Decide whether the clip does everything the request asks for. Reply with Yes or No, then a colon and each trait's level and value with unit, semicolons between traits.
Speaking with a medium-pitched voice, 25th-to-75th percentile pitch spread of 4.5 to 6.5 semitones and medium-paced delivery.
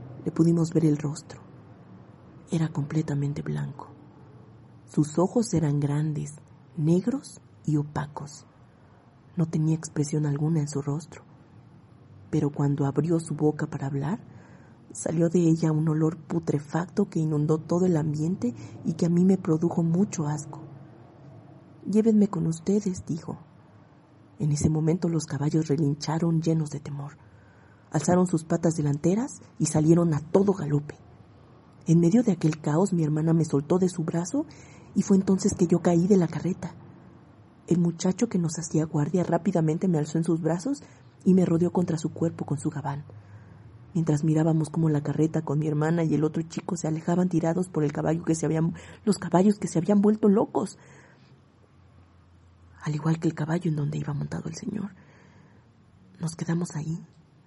No: medium, 155 Hz; average, 2.7 semitones; average, 160 wpm